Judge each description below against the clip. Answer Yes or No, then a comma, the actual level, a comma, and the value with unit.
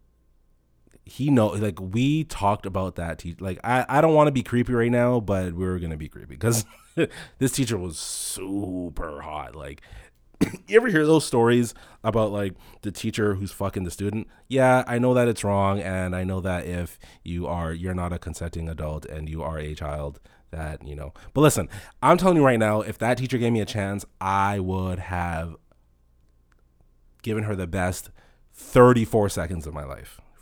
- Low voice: Yes, very low, 95 Hz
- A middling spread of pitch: No, wide, 5.7 semitones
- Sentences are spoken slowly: No, average, 185 wpm